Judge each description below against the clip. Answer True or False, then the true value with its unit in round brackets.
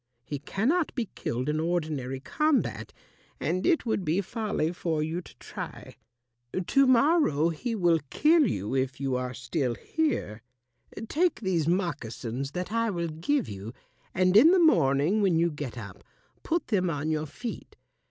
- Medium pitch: True (170 Hz)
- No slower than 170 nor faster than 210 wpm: False (160 wpm)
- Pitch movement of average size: False (8.4 semitones)